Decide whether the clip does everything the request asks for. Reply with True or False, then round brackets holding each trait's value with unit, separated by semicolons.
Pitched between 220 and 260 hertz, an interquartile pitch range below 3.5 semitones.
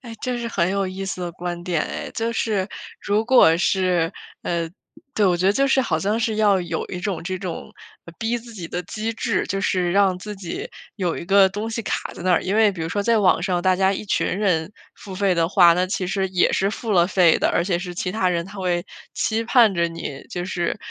False (190 Hz; 3.1 semitones)